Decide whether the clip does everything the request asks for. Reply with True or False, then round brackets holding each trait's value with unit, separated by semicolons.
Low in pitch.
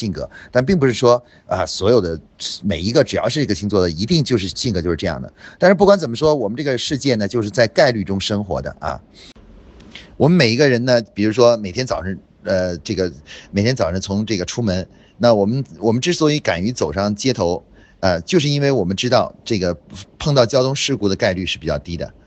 True (110 Hz)